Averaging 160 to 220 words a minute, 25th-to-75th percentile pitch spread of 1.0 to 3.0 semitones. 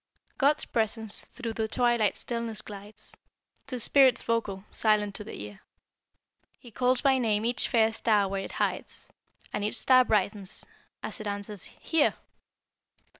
No: average, 145 wpm; average, 2.7 semitones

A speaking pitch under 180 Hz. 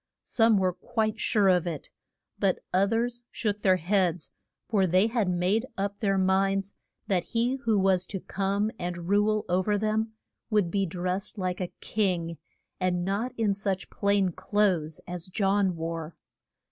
No: high, 195 Hz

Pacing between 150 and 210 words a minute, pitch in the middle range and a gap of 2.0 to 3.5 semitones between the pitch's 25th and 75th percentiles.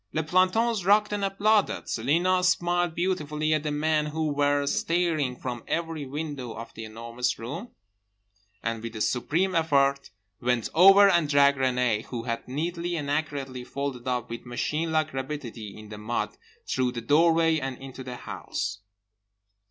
No: average, 160 wpm; medium, 145 Hz; average, 5.2 semitones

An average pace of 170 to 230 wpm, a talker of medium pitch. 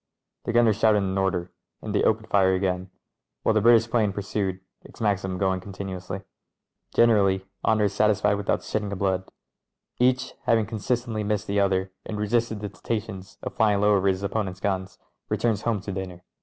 No: average, 180 wpm; low, 100 Hz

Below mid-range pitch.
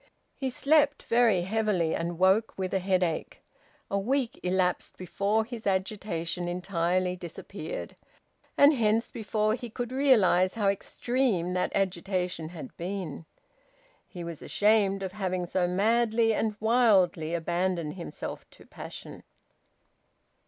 No: high, 195 Hz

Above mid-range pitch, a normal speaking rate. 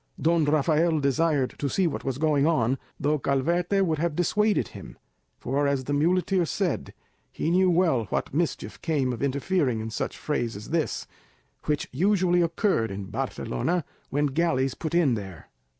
No: medium, 150 Hz; average, 165 wpm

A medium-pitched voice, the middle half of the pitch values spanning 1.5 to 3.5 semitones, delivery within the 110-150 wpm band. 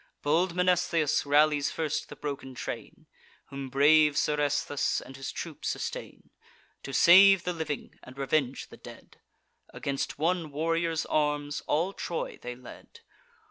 Yes: medium, 150 Hz; average, 2.9 semitones; slow, 135 wpm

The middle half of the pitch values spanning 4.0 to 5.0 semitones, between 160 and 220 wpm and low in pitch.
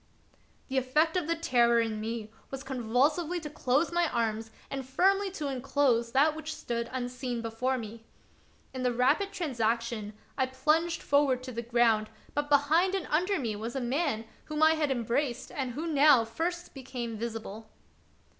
No: average, 4.6 semitones; average, 165 wpm; very high, 260 Hz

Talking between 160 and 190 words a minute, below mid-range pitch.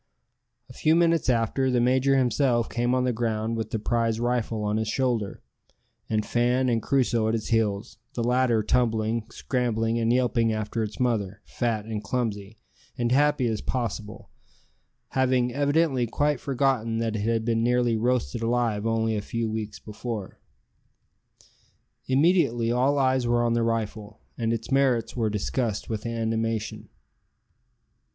No: average, 150 wpm; low, 115 Hz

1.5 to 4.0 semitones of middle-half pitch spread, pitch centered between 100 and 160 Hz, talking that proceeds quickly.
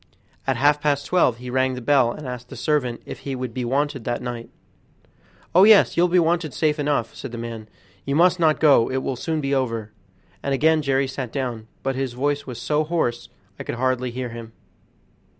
Yes: average, 3.5 semitones; low, 135 Hz; fast, 210 wpm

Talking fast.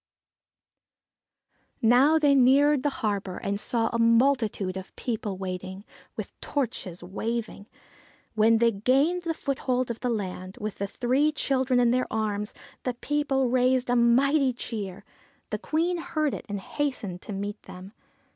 No: average, 145 wpm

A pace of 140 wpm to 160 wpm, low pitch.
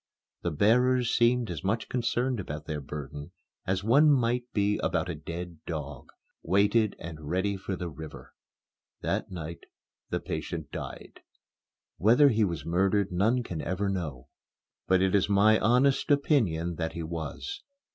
Yes: average, 150 wpm; very low, 95 Hz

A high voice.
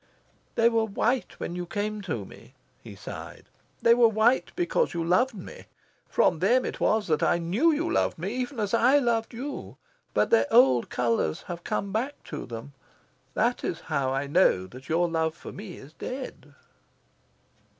Yes: high, 205 Hz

